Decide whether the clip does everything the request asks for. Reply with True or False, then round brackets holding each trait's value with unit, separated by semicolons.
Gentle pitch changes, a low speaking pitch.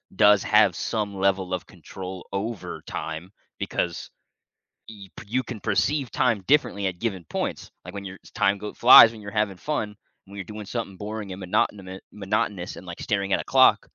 True (2.2 semitones; 100 Hz)